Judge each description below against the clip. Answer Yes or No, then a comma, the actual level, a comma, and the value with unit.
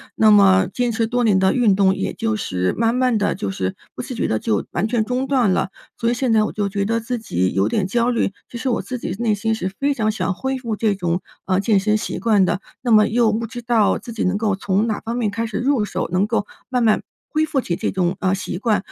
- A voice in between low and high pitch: No, high, 220 Hz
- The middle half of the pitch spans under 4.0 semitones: Yes, average, 3.5 semitones